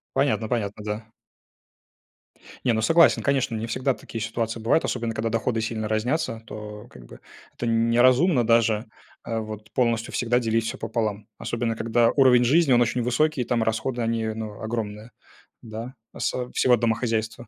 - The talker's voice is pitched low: Yes, low, 115 Hz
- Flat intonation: Yes, narrow, 1.9 semitones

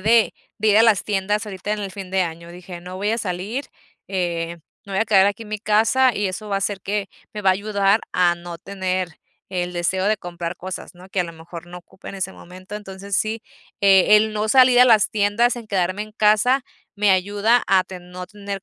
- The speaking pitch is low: No, high, 195 Hz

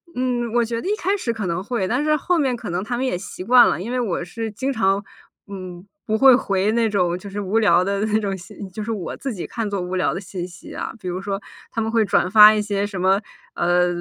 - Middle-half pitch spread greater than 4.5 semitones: No, average, 4.0 semitones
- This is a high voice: Yes, high, 205 Hz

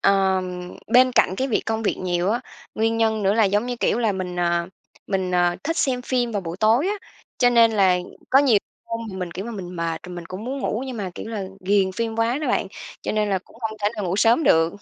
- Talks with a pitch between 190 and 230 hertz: Yes, high, 210 Hz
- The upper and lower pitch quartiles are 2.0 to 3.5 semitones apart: No, average, 4.1 semitones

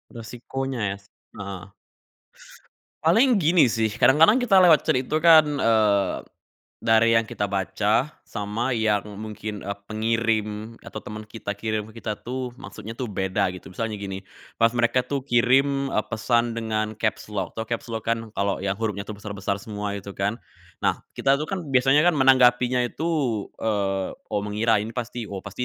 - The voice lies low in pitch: Yes, low, 110 Hz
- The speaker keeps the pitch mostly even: No, average, 3.5 semitones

